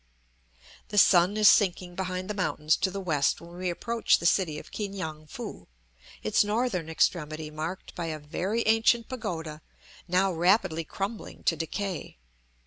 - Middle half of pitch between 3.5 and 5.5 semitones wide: Yes, average, 3.9 semitones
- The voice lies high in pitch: No, medium, 180 Hz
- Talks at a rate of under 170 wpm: Yes, average, 155 wpm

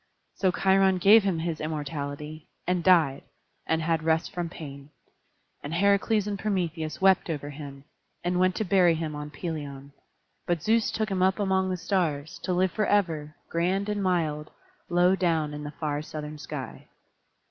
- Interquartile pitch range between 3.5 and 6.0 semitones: Yes, average, 3.9 semitones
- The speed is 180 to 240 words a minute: No, average, 165 wpm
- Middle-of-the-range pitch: Yes, medium, 170 Hz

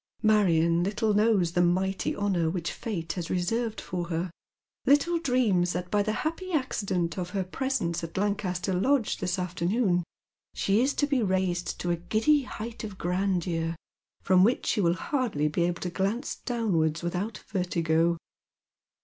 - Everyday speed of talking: Yes, average, 165 wpm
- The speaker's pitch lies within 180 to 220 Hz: Yes, medium, 185 Hz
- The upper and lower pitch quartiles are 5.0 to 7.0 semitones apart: No, average, 4.2 semitones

